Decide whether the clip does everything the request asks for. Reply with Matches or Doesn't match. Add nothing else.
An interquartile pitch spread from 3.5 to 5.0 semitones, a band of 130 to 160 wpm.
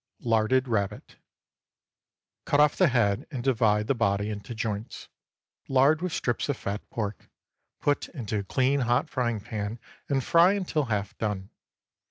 Matches